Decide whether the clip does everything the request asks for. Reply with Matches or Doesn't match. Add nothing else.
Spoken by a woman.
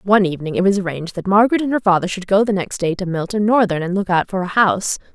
Matches